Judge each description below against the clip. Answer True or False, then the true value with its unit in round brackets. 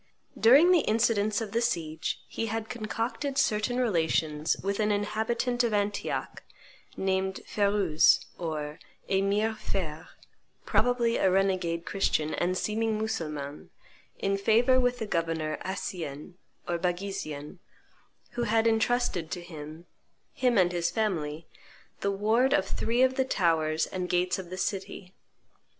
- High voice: True (195 Hz)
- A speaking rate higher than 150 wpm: False (135 wpm)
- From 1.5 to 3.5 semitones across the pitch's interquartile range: False (5.0 semitones)